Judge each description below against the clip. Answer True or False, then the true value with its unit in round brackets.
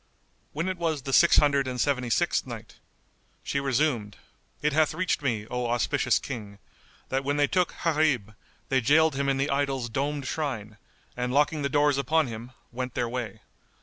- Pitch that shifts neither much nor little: True (3.3 semitones)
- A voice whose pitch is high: False (135 Hz)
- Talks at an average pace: True (180 wpm)